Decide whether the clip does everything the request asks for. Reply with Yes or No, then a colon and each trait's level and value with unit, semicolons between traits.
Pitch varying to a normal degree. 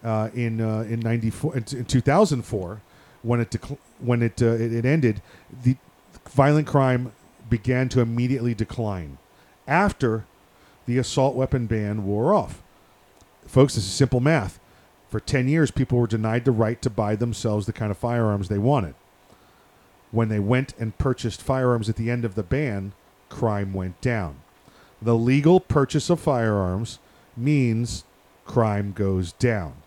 Yes: average, 3.7 semitones